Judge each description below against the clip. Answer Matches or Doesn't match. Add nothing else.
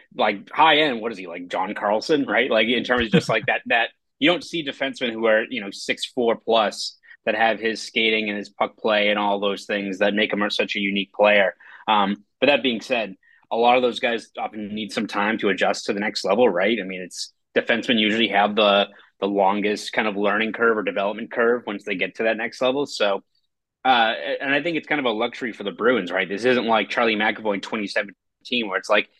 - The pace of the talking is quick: Matches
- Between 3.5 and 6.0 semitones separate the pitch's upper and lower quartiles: Doesn't match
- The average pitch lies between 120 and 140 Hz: Doesn't match